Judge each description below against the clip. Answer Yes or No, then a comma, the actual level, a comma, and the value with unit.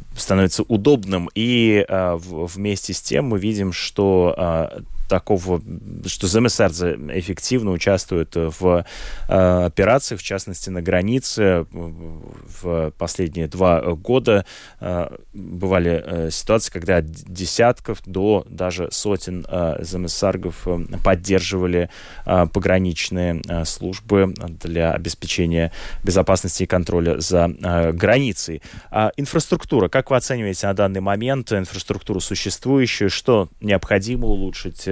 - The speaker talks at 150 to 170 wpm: No, average, 115 wpm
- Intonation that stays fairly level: No, average, 3.0 semitones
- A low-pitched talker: Yes, very low, 95 Hz